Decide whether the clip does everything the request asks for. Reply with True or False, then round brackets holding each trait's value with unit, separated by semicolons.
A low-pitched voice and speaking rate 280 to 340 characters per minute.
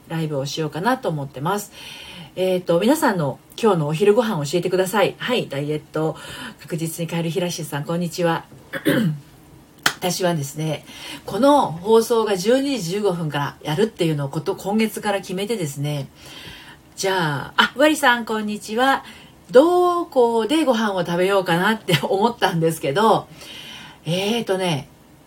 False (185 Hz; 325 characters per minute)